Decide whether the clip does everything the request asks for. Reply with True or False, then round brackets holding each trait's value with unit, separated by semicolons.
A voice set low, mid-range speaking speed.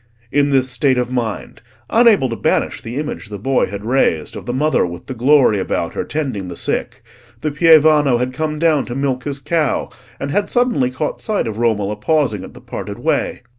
True (130 Hz; 195 wpm)